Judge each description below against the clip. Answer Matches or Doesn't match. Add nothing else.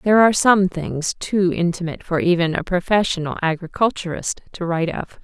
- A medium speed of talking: Matches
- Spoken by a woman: Matches